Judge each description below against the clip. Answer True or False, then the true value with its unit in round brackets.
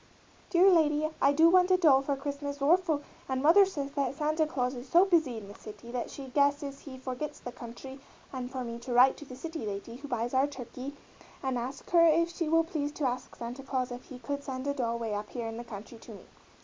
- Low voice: False (275 Hz)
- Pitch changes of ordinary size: True (3.5 semitones)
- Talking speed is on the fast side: True (245 wpm)